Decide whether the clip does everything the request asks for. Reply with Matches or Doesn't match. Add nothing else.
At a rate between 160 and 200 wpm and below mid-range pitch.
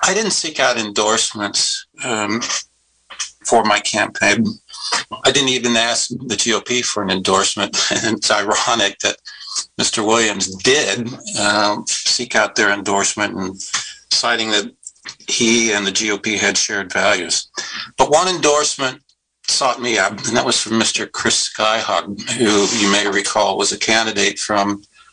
Doesn't match